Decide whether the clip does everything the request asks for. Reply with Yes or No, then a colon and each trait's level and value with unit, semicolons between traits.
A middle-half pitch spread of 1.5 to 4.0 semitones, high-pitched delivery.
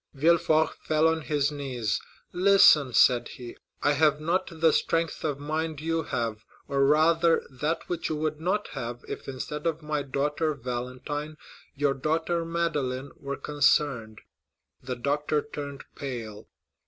No: average, 3.1 semitones; medium, 150 Hz